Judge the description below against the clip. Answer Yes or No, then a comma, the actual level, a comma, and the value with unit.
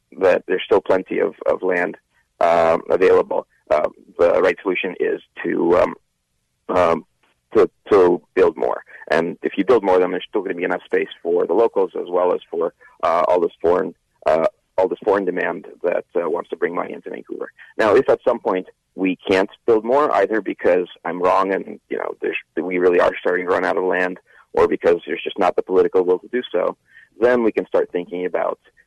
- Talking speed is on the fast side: Yes, fast, 210 wpm